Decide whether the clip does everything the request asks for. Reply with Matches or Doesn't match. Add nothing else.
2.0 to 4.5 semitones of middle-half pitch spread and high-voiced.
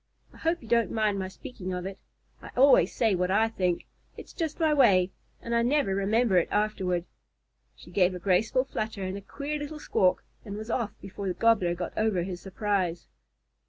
Matches